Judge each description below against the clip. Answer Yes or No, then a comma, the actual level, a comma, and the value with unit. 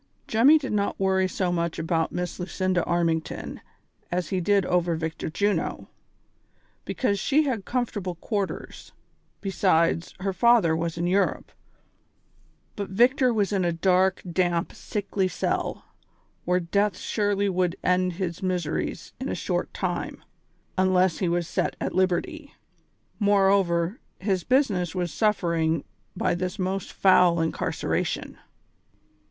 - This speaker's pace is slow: Yes, slow, 130 wpm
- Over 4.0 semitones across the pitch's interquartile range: No, average, 2.7 semitones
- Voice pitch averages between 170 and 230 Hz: Yes, medium, 185 Hz